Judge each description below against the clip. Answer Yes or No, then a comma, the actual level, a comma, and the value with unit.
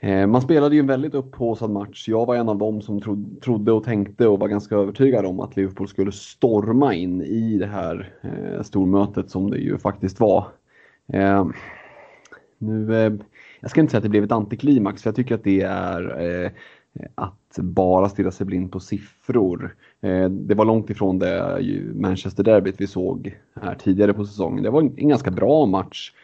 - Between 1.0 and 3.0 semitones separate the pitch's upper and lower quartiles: Yes, average, 2.7 semitones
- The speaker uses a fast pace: No, average, 175 wpm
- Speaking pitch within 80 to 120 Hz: Yes, low, 100 Hz